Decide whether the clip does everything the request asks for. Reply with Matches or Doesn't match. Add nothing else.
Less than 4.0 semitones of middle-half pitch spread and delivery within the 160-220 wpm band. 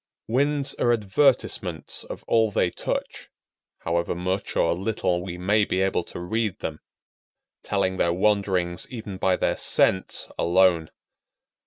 Doesn't match